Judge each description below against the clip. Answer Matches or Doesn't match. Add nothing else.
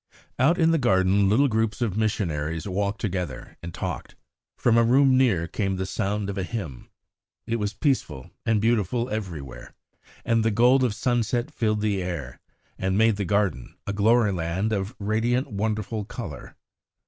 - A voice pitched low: Matches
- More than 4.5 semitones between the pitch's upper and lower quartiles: Doesn't match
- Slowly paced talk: Doesn't match